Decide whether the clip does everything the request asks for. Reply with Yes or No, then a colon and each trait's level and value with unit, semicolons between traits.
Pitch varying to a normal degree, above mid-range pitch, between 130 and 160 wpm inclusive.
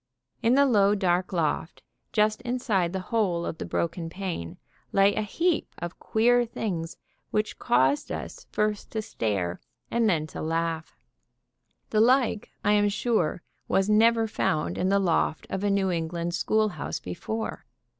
Yes: average, 4.5 semitones; high, 195 Hz; average, 150 wpm